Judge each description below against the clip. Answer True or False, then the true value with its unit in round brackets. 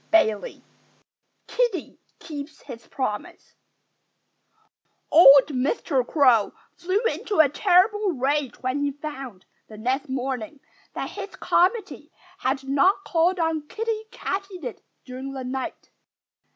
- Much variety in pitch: True (5.9 semitones)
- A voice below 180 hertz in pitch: False (290 Hz)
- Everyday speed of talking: False (110 wpm)